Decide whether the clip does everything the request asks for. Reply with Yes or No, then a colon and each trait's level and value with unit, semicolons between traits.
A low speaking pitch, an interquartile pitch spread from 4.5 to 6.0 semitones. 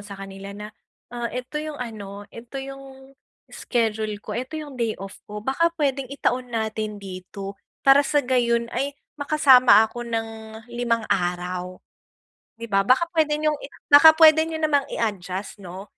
No: high, 235 Hz; average, 5.1 semitones